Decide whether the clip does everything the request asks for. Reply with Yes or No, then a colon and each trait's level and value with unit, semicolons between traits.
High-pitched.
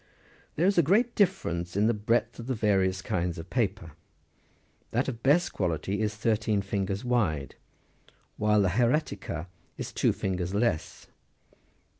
No: low, 105 Hz